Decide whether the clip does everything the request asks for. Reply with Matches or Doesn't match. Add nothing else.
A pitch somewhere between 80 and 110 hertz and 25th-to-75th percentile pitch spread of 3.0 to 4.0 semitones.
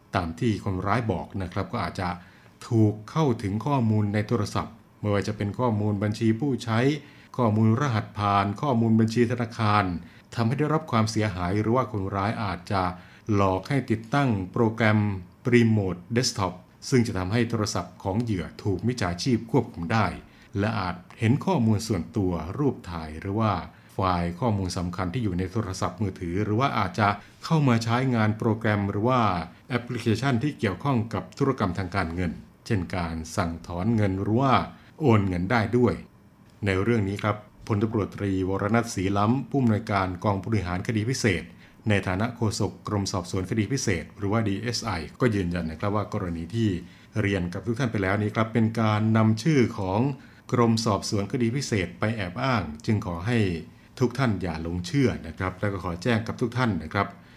Matches